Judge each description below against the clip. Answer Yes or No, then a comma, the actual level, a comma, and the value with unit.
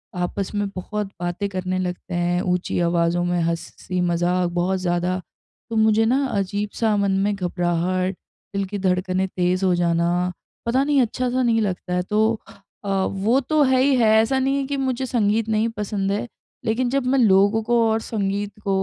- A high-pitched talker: Yes, high, 200 Hz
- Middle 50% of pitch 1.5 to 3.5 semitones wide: No, average, 3.9 semitones